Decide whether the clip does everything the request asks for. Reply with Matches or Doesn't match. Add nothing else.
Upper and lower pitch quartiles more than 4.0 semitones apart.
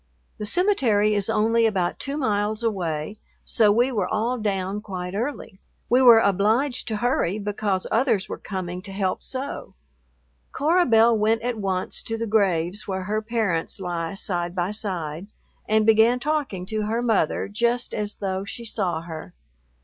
Doesn't match